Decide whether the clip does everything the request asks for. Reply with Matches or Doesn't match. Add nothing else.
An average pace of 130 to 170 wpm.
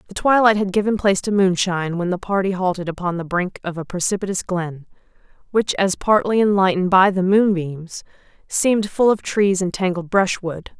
Doesn't match